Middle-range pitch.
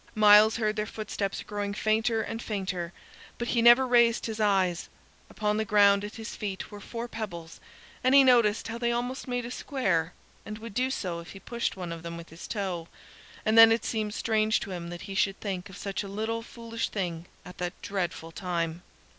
No: high, 210 Hz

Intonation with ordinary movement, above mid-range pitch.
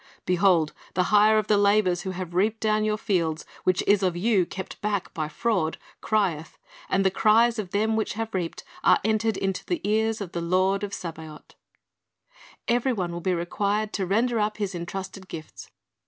Yes: average, 3.2 semitones; high, 195 Hz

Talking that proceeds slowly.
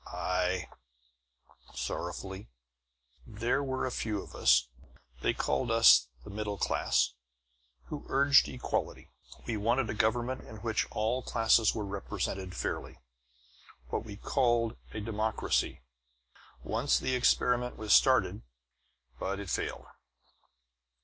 Yes: slow, 115 wpm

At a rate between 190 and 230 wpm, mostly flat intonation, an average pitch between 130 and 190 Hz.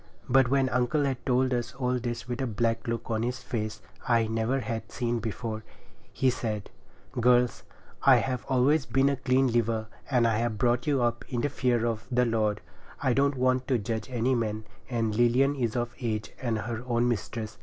No: average, 195 wpm; narrow, 2.1 semitones; low, 120 Hz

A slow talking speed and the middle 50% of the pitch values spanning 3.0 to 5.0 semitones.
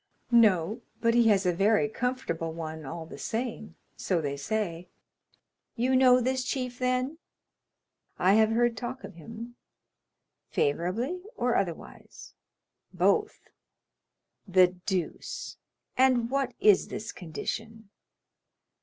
No: slow, 110 wpm; wide, 5.6 semitones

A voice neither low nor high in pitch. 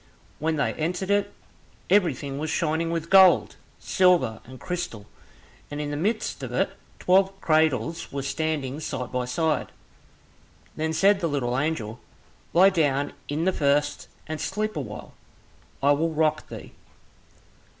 Yes: medium, 155 Hz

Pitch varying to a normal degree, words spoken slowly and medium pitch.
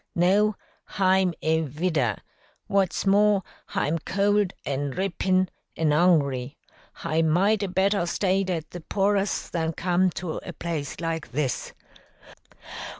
Yes: average, 3.5 semitones; slow, 130 wpm; medium, 175 Hz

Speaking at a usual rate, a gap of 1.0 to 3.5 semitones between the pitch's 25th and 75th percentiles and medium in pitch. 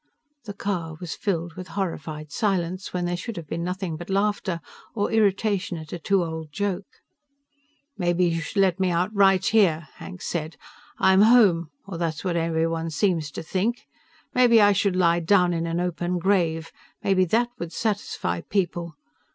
Yes: average, 170 wpm; average, 3.1 semitones; medium, 180 Hz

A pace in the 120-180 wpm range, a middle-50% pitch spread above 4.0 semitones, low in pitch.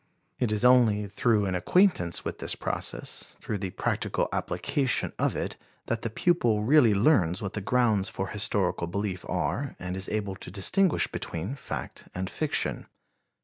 Yes: average, 160 wpm; average, 4.5 semitones; low, 105 Hz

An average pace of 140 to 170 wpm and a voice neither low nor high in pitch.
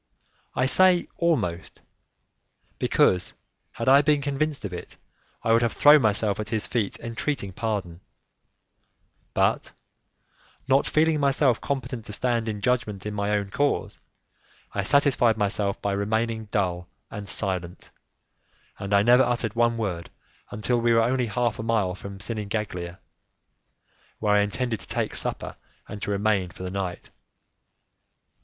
No: average, 145 wpm; low, 110 Hz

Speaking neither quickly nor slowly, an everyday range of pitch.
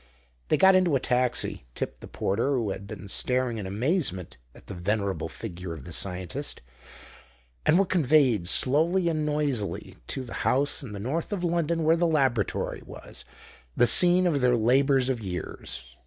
No: average, 170 wpm; wide, 7.7 semitones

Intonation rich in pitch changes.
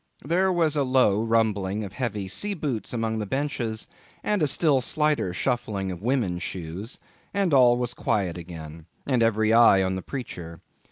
Yes: wide, 6.0 semitones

